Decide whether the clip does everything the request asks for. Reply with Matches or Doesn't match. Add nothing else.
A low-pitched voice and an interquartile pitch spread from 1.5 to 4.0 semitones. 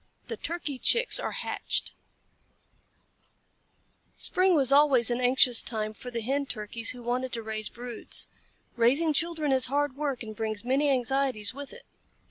Doesn't match